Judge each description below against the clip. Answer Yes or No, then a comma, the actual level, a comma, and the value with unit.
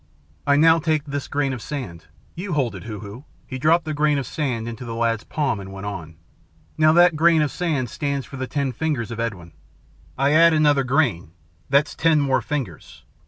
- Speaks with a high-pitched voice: No, medium, 140 Hz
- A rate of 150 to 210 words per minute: Yes, fast, 205 wpm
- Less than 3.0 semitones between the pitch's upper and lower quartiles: No, average, 4.8 semitones